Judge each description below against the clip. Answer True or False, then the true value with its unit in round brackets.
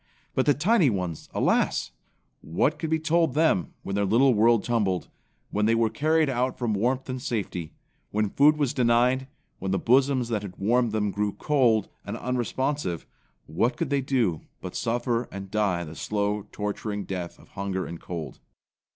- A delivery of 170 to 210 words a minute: True (175 wpm)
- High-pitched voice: False (115 Hz)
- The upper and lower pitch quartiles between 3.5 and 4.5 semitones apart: False (4.9 semitones)